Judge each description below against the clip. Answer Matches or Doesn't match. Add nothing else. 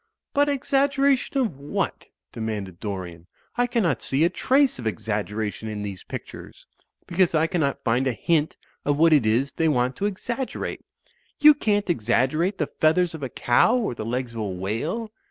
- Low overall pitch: Doesn't match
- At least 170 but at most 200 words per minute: Matches